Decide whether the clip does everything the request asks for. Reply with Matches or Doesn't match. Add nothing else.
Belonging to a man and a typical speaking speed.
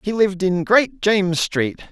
Matches